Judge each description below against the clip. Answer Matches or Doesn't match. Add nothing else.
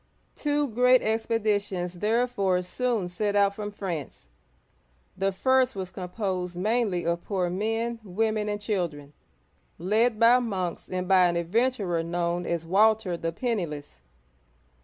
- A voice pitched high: Matches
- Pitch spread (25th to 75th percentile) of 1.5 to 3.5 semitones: Doesn't match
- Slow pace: Matches